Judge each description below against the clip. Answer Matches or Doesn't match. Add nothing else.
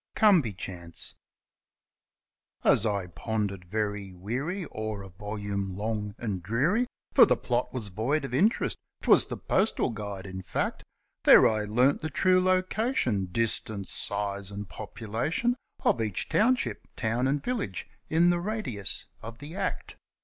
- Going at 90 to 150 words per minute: Matches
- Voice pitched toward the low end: Matches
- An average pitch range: Doesn't match